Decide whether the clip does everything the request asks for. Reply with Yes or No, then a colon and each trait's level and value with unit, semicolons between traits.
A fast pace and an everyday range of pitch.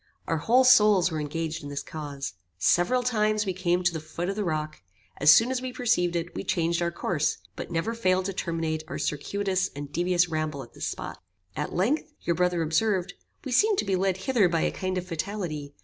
Yes: fast, 215 wpm; average, 4.3 semitones